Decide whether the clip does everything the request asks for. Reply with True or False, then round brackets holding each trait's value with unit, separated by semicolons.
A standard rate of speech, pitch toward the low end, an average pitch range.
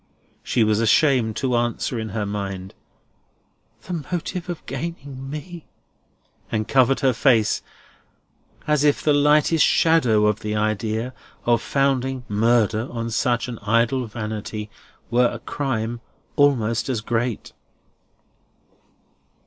False (120 wpm; 120 Hz; 4.0 semitones)